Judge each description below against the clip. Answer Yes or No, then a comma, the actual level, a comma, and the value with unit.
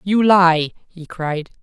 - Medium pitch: Yes, medium, 175 Hz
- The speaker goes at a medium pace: Yes, average, 145 wpm